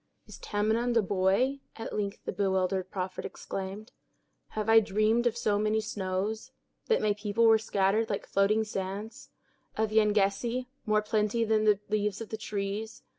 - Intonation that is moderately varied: No, narrow, 1.8 semitones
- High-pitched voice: Yes, high, 210 Hz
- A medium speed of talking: Yes, average, 150 wpm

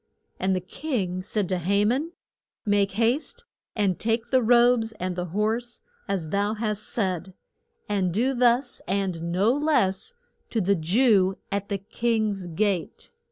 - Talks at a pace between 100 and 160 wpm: Yes, average, 150 wpm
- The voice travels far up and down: No, average, 3.9 semitones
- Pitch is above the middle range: Yes, high, 205 Hz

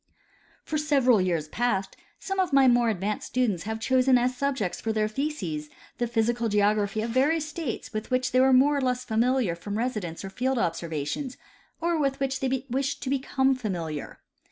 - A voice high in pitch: Yes, high, 245 Hz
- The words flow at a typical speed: Yes, average, 180 wpm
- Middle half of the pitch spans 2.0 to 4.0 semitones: No, average, 4.4 semitones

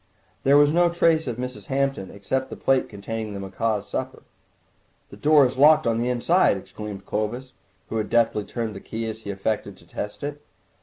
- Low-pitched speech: Yes, low, 115 Hz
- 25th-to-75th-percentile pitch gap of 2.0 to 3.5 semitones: No, average, 4.6 semitones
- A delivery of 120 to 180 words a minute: No, average, 195 wpm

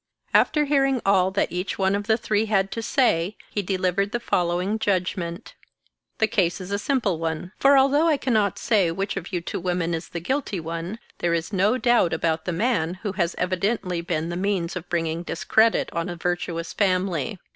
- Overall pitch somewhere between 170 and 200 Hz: Yes, medium, 185 Hz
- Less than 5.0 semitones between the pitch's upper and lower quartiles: Yes, average, 4.1 semitones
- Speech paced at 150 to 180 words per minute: No, average, 200 wpm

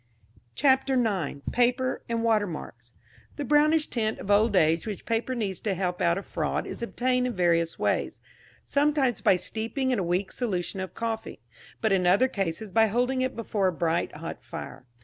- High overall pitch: Yes, high, 220 Hz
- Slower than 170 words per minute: No, average, 180 wpm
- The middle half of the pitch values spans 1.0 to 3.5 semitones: No, wide, 5.5 semitones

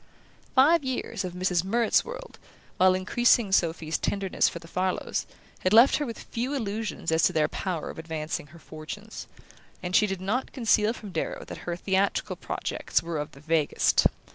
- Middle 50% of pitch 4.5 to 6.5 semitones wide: Yes, average, 5.3 semitones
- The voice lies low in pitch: No, high, 190 Hz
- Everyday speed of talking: Yes, average, 175 wpm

